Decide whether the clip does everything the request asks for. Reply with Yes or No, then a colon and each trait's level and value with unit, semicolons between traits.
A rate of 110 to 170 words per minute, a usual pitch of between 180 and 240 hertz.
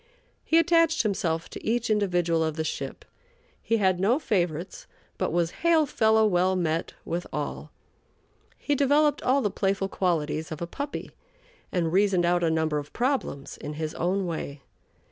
Yes: average, 165 wpm; medium, 185 Hz